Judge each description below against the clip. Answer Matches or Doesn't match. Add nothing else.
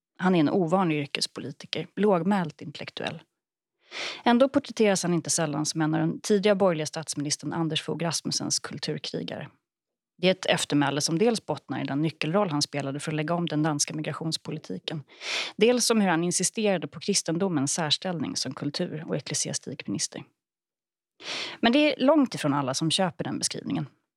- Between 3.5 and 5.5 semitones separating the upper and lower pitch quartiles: Matches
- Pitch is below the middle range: Doesn't match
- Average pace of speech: Matches